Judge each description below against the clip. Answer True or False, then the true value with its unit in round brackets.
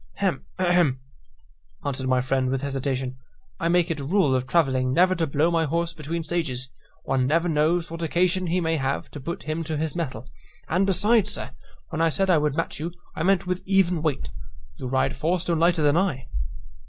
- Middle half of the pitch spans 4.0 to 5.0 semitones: True (4.3 semitones)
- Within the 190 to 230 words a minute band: True (205 wpm)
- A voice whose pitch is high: False (160 Hz)